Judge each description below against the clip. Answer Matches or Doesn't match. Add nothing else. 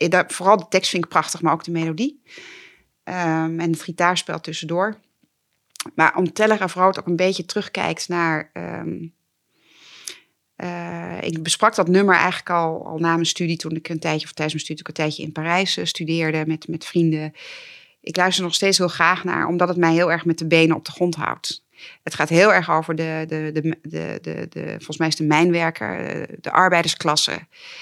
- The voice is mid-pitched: Matches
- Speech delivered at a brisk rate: Matches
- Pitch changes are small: Matches